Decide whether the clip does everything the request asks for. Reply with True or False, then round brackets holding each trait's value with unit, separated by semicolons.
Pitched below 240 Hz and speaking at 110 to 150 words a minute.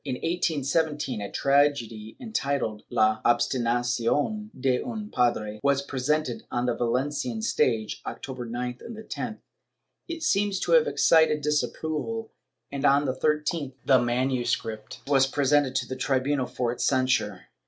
True (135 Hz; 140 wpm)